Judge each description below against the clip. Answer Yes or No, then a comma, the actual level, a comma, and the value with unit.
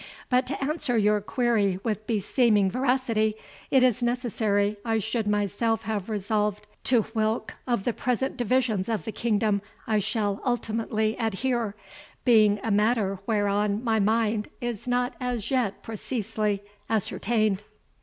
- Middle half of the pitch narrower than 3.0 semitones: Yes, narrow, 2.6 semitones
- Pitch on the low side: No, high, 220 Hz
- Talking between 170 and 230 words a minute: No, slow, 135 wpm